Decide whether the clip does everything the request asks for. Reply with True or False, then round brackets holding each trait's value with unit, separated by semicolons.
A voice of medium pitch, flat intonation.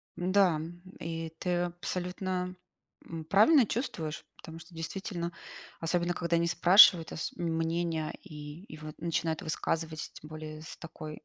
True (165 Hz; 2.0 semitones)